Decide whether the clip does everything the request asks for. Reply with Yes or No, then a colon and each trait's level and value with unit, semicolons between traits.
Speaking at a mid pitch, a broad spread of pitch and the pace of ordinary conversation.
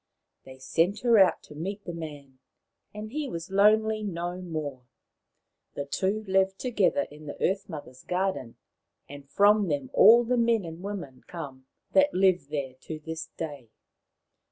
Yes: medium, 175 Hz; wide, 6.0 semitones; average, 160 wpm